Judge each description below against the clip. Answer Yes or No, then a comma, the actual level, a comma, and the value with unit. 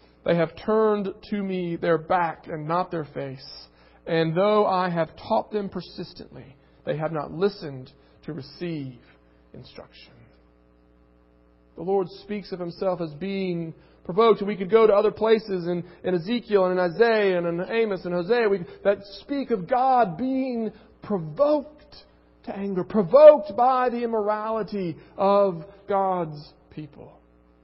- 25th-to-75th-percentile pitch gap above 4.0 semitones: Yes, average, 4.7 semitones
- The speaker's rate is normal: Yes, average, 145 wpm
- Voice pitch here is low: No, medium, 185 Hz